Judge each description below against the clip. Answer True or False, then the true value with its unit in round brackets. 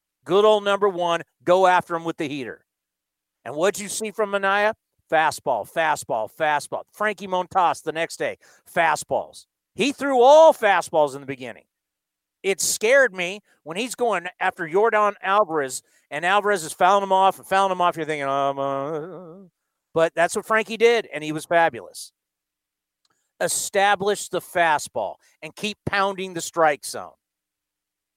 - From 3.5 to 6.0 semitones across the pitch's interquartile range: True (5.4 semitones)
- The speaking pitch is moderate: True (180 Hz)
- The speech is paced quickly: False (155 wpm)